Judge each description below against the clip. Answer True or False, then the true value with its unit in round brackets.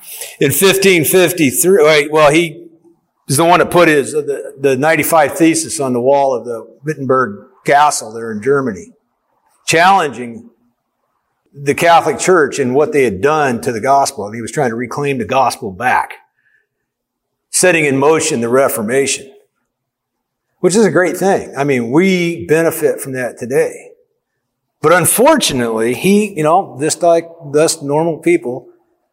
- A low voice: False (160 Hz)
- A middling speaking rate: True (155 wpm)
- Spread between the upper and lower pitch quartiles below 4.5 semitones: False (5.6 semitones)